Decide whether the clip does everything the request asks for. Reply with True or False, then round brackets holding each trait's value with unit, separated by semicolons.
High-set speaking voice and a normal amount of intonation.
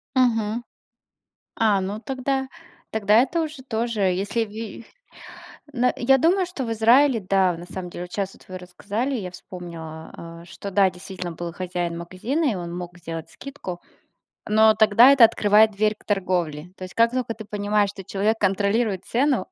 True (205 Hz; 4.4 semitones)